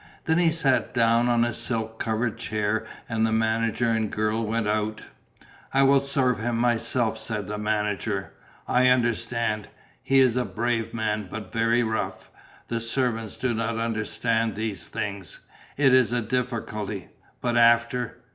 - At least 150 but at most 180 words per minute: Yes, average, 155 wpm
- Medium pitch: No, low, 115 Hz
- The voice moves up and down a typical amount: No, narrow, 1.9 semitones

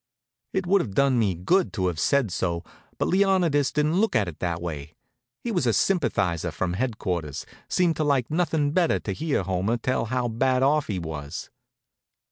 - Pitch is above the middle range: No, low, 120 Hz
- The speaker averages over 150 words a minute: Yes, average, 190 wpm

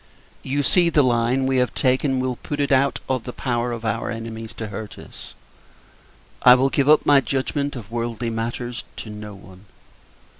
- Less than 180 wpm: No, average, 185 wpm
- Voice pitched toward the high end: No, low, 125 Hz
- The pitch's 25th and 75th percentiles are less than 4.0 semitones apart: Yes, average, 2.8 semitones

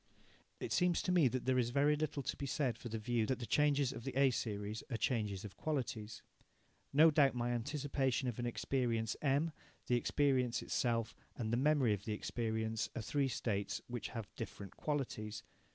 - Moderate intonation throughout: Yes, average, 3.8 semitones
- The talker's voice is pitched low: Yes, low, 120 Hz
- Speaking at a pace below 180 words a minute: No, average, 190 wpm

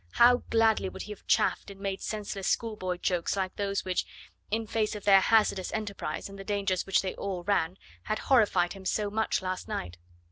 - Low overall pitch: No, high, 200 Hz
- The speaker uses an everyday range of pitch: No, narrow, 2.3 semitones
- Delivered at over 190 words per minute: Yes, average, 200 wpm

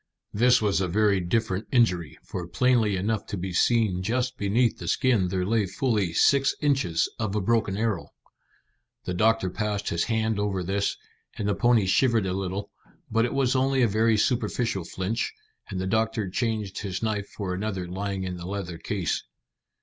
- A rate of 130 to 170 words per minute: No, average, 180 wpm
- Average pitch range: Yes, average, 3.4 semitones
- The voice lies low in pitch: Yes, low, 105 Hz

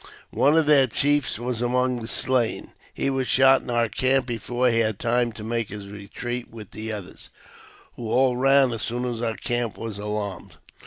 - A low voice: Yes, low, 120 Hz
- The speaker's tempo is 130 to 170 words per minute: No, average, 195 wpm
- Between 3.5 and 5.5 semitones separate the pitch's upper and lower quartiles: No, average, 2.7 semitones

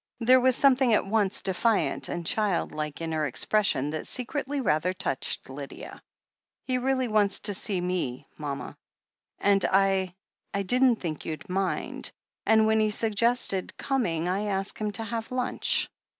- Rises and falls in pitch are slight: No, average, 4.6 semitones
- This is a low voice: No, high, 200 Hz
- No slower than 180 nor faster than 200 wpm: No, average, 155 wpm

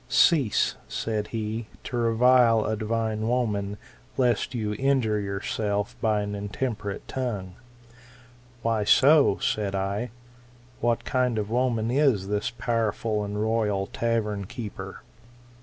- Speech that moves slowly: Yes, slow, 125 wpm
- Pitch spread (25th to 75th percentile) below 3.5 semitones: Yes, narrow, 2.6 semitones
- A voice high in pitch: No, low, 110 Hz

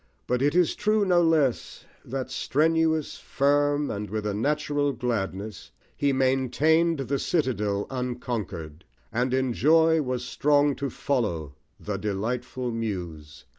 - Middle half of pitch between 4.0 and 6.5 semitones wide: Yes, wide, 5.4 semitones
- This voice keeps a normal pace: No, slow, 130 wpm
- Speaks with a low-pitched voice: Yes, low, 130 Hz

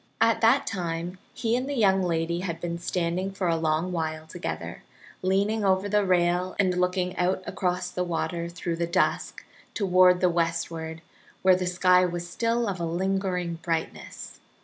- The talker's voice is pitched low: No, medium, 180 Hz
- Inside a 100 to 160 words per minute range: No, average, 170 wpm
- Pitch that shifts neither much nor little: No, narrow, 2.0 semitones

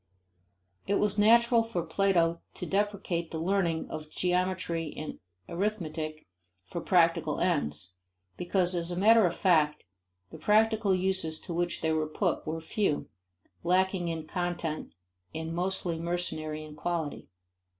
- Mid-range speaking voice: Yes, medium, 175 Hz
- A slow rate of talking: Yes, slow, 130 wpm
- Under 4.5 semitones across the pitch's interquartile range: Yes, average, 3.0 semitones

